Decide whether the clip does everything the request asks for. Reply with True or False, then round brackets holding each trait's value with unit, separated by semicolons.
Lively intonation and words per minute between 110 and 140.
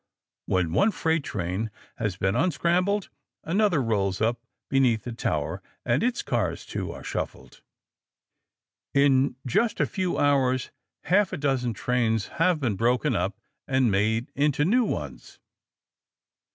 True (6.8 semitones; 135 wpm)